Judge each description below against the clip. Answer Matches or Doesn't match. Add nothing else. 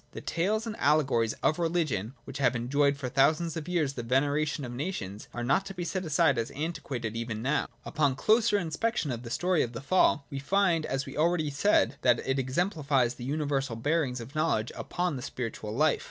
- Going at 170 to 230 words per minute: Matches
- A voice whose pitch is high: Doesn't match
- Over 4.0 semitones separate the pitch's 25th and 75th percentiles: Matches